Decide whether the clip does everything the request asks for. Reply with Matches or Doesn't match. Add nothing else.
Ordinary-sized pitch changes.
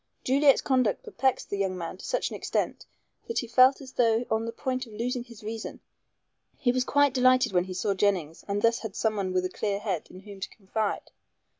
Matches